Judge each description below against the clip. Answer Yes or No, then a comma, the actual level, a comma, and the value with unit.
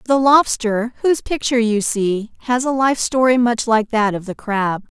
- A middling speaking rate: Yes, average, 190 wpm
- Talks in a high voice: Yes, high, 235 Hz